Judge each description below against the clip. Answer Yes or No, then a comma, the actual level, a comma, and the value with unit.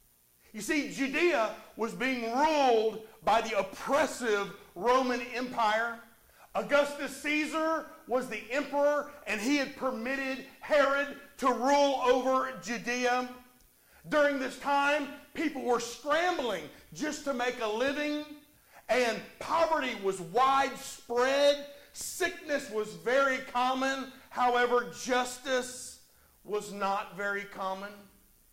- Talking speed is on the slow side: Yes, slow, 105 wpm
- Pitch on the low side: No, very high, 260 Hz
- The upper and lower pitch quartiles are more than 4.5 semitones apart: No, average, 4.1 semitones